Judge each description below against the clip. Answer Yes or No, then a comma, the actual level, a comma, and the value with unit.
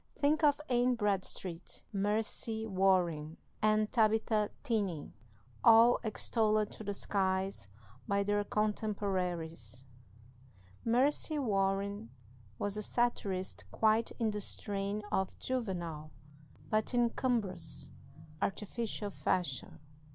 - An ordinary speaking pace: No, slow, 100 wpm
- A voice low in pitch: No, high, 205 Hz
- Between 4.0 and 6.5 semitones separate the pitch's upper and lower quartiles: No, average, 3.0 semitones